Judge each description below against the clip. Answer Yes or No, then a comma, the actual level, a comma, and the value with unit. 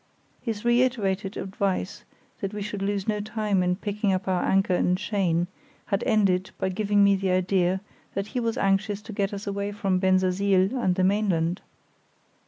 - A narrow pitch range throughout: Yes, narrow, 1.8 semitones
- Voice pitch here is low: No, high, 195 Hz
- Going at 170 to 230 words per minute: Yes, average, 175 wpm